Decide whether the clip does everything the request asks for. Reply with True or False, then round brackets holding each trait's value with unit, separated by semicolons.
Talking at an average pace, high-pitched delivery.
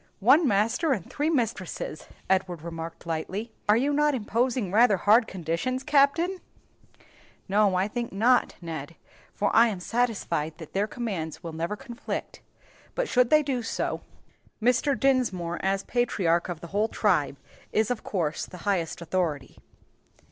True (150 wpm; 210 Hz)